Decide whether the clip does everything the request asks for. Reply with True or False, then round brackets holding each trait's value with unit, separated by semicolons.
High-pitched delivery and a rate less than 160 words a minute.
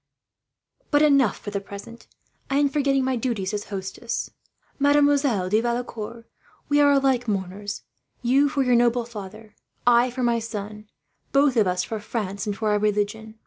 False (230 Hz; 165 wpm)